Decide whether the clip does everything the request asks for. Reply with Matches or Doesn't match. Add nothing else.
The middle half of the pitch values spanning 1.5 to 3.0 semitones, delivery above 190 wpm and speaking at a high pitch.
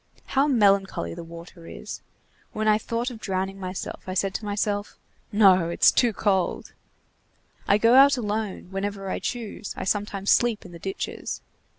Doesn't match